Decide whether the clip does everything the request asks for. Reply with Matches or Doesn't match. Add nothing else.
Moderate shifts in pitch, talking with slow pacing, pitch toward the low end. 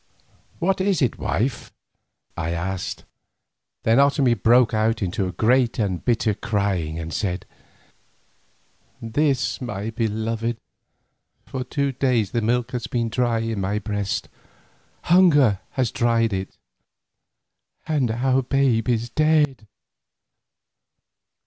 Matches